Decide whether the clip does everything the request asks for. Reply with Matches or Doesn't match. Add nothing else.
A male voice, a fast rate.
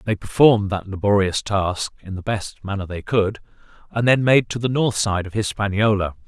Doesn't match